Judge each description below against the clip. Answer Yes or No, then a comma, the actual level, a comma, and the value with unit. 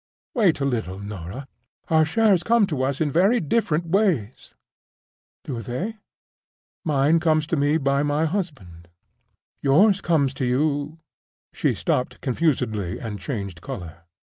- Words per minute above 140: No, slow, 135 wpm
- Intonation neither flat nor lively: No, wide, 5.7 semitones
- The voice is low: No, medium, 145 Hz